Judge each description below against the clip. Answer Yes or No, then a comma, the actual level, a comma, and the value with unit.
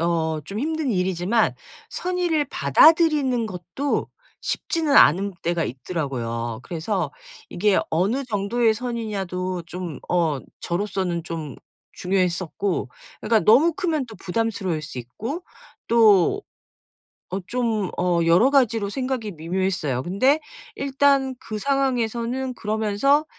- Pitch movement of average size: No, wide, 6.8 semitones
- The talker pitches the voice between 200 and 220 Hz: Yes, high, 205 Hz